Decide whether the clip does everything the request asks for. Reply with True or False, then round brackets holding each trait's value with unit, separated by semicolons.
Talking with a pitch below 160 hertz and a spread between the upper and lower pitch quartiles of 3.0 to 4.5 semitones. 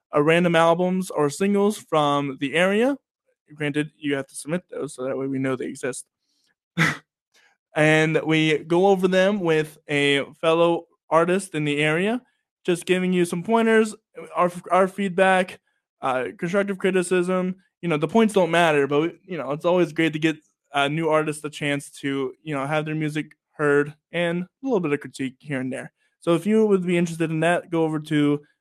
False (165 Hz; 3.6 semitones)